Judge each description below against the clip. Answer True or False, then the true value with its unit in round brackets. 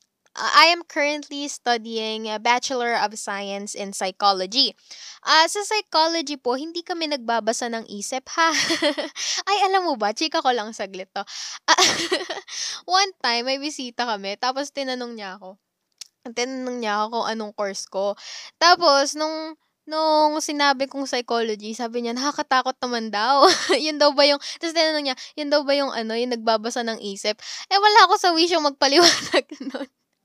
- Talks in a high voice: True (270 Hz)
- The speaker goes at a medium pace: False (160 wpm)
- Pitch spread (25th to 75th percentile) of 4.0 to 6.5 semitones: True (5.4 semitones)